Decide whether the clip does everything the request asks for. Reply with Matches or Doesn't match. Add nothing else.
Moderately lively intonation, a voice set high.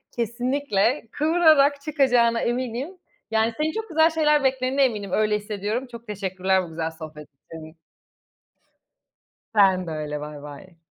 Doesn't match